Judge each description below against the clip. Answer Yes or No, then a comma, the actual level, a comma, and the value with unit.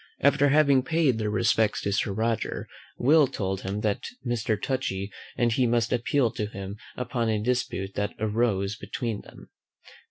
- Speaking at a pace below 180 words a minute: Yes, average, 160 wpm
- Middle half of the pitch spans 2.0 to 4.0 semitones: Yes, average, 3.5 semitones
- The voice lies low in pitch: Yes, low, 115 Hz